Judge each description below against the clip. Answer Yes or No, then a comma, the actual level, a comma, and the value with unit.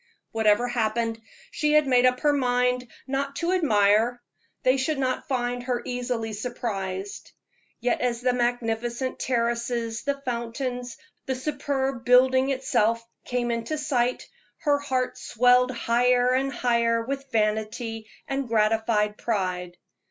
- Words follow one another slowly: Yes, slow, 130 wpm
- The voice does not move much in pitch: Yes, narrow, 2.3 semitones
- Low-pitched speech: No, high, 245 Hz